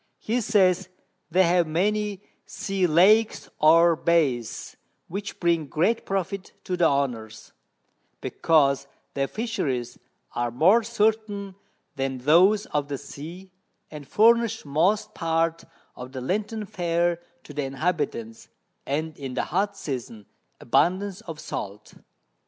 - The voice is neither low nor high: Yes, medium, 170 Hz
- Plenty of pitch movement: Yes, wide, 6.1 semitones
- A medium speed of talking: No, slow, 125 wpm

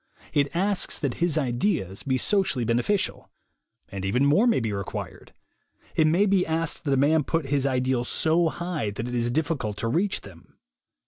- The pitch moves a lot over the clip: Yes, wide, 5.7 semitones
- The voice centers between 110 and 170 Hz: Yes, medium, 140 Hz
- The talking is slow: No, average, 180 wpm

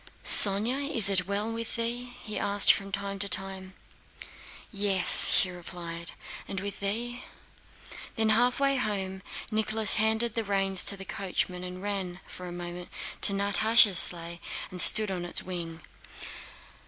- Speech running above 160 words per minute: No, average, 145 wpm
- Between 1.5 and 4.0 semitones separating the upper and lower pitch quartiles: Yes, average, 3.1 semitones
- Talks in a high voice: Yes, high, 200 Hz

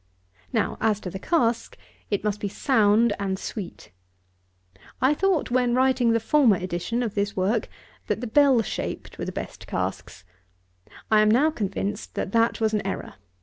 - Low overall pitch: No, high, 220 Hz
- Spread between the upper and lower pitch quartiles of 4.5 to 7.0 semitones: No, average, 3.4 semitones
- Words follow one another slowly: No, average, 170 wpm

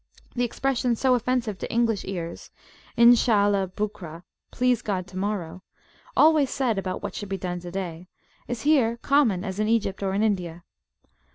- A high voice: Yes, high, 205 Hz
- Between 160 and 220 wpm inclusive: No, average, 150 wpm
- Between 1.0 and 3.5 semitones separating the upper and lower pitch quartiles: No, average, 4.5 semitones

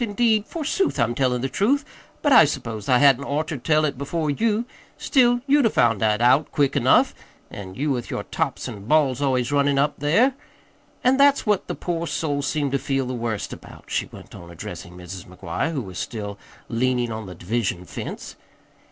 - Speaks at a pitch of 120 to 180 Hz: Yes, medium, 140 Hz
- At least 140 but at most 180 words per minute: No, average, 195 wpm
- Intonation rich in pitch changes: Yes, wide, 6.4 semitones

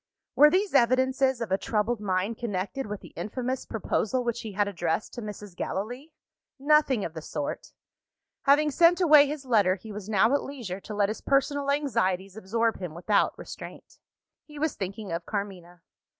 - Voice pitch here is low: No, high, 220 Hz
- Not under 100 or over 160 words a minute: No, average, 175 wpm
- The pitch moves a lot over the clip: Yes, wide, 5.8 semitones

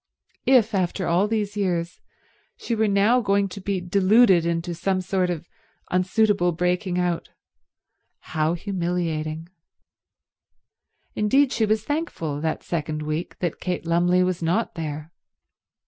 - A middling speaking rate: No, slow, 130 wpm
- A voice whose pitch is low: No, medium, 180 Hz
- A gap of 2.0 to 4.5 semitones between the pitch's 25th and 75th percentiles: Yes, average, 3.1 semitones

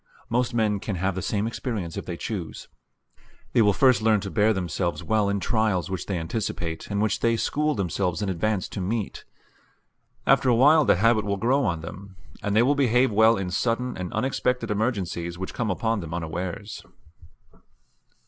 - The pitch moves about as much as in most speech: Yes, average, 3.8 semitones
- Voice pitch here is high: No, low, 105 Hz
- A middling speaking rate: Yes, average, 185 wpm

